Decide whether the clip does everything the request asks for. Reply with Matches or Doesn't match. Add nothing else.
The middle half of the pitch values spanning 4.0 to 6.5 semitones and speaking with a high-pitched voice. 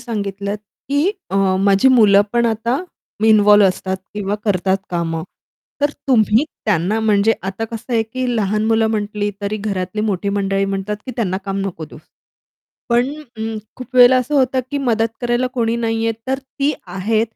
Doesn't match